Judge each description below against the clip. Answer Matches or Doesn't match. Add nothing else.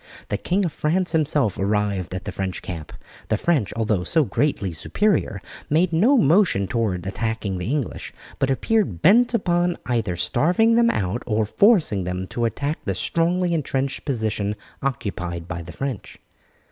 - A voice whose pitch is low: Matches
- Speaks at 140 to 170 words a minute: Matches